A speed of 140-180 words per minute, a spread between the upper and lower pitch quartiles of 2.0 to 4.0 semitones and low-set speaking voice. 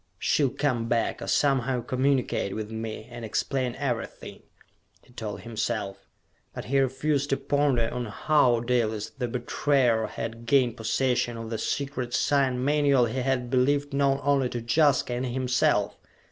Yes: average, 150 wpm; average, 3.0 semitones; low, 125 Hz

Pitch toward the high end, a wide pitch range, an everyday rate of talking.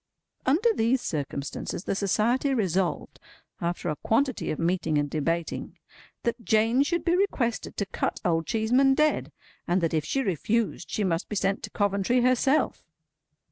Yes: high, 215 Hz; wide, 6.9 semitones; average, 155 wpm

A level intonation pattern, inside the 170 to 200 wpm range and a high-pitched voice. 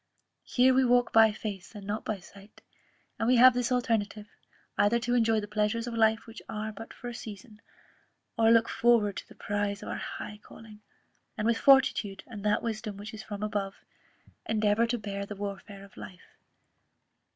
Yes: narrow, 2.1 semitones; average, 185 wpm; high, 215 Hz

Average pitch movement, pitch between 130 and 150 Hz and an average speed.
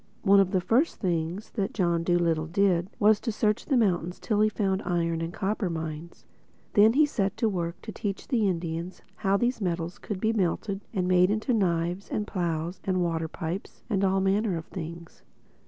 No: average, 3.6 semitones; high, 190 Hz; average, 190 wpm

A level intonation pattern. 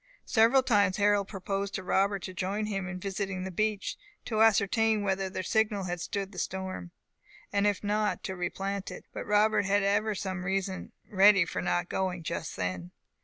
Yes: narrow, 1.7 semitones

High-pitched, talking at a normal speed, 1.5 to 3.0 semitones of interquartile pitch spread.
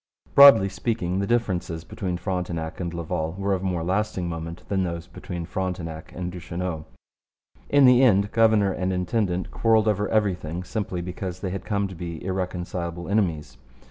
No: very low, 90 Hz; average, 160 wpm; narrow, 2.6 semitones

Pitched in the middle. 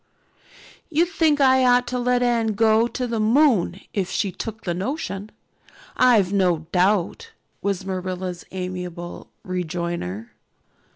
No: high, 200 Hz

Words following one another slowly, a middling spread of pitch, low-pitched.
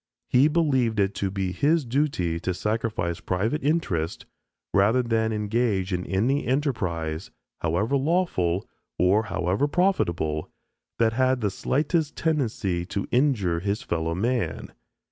No: slow, 125 wpm; wide, 6.7 semitones; low, 110 Hz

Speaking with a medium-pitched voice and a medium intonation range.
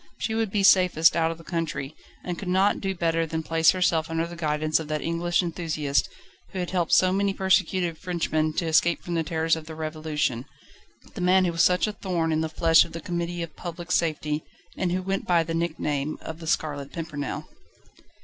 No: medium, 165 Hz; narrow, 2.3 semitones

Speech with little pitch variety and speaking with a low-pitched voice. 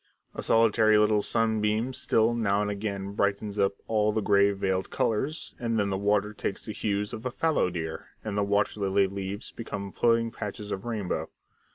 Yes: narrow, 1.9 semitones; low, 105 Hz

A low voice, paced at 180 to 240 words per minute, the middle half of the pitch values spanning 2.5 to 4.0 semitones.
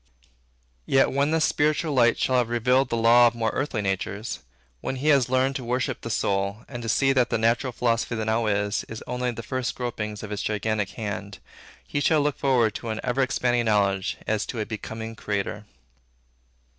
Yes: low, 115 Hz; average, 195 wpm; average, 3.0 semitones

